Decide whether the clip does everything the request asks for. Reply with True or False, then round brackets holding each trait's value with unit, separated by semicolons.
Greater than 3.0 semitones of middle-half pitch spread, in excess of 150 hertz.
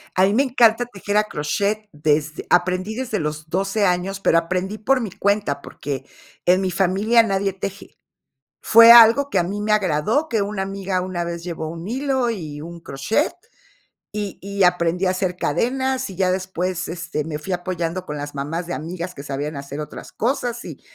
True (4.1 semitones; 185 Hz)